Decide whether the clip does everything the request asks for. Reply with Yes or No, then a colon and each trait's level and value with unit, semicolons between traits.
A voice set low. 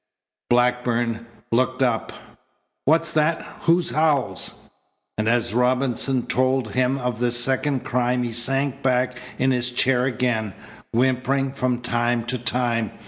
Yes: low, 125 Hz